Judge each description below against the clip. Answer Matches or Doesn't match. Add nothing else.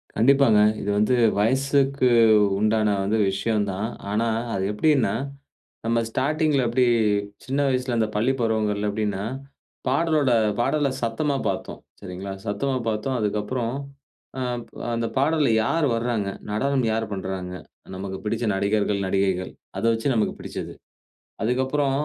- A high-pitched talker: Doesn't match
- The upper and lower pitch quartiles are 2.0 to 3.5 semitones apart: Doesn't match